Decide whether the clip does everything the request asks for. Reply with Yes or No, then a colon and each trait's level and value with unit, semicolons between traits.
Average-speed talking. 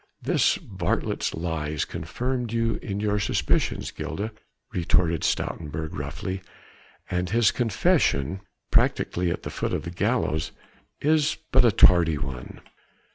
No: slow, 125 wpm